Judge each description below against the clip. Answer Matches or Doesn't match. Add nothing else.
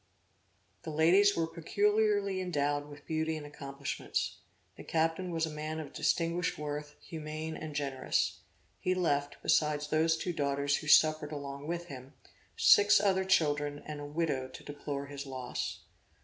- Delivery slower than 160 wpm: Matches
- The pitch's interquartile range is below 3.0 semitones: Matches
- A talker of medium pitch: Matches